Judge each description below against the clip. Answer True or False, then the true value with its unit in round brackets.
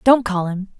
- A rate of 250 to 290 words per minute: False (225 wpm)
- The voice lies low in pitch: False (205 Hz)